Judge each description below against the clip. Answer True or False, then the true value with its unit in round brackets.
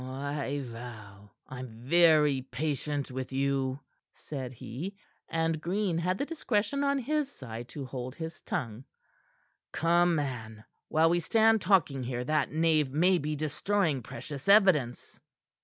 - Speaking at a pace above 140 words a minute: False (135 wpm)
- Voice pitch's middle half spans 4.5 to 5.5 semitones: True (5.1 semitones)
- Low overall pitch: False (150 Hz)